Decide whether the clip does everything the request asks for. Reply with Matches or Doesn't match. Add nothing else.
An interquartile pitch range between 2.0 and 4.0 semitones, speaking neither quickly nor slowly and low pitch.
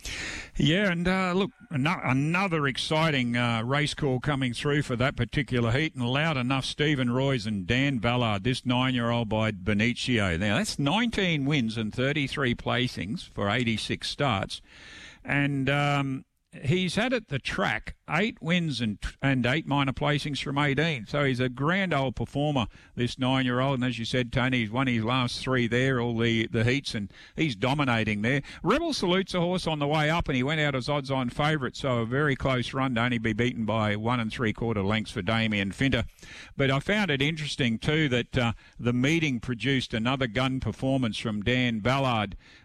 Matches